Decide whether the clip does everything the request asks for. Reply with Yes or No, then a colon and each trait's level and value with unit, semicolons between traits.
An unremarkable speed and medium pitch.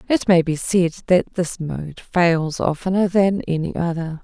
Yes: average, 170 wpm; medium, 175 Hz